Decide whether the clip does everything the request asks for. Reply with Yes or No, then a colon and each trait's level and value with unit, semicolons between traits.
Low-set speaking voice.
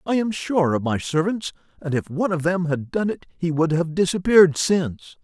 No: medium, 170 Hz